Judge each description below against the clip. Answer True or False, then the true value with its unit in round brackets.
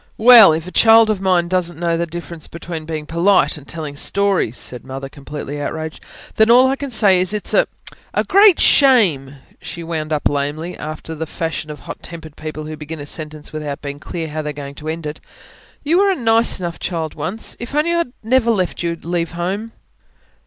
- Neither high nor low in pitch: True (170 Hz)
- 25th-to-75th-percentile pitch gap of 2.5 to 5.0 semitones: False (5.4 semitones)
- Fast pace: True (210 wpm)